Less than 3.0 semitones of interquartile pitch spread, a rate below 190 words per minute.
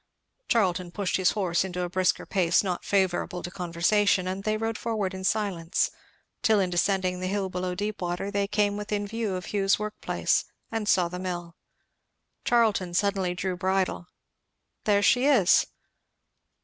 Yes: narrow, 2.5 semitones; average, 150 wpm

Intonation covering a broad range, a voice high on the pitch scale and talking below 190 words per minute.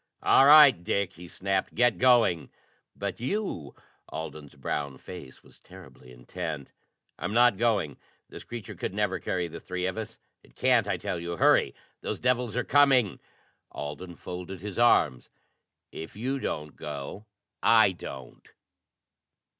No: wide, 6.5 semitones; very low, 95 Hz; average, 145 wpm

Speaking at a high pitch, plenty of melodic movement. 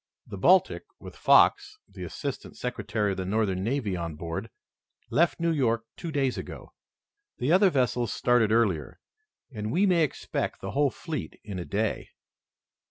No: low, 115 Hz; wide, 6.0 semitones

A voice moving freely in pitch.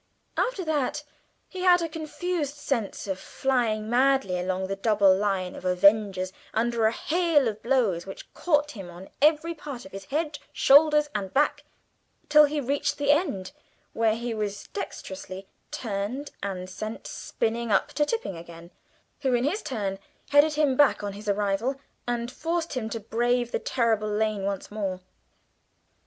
Yes: wide, 6.7 semitones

